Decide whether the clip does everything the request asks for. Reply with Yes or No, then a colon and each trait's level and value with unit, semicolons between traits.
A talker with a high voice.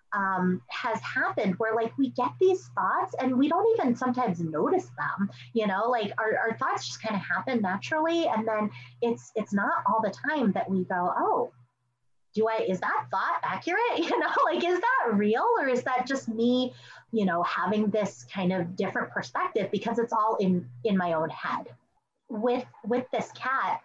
Yes: high, 220 Hz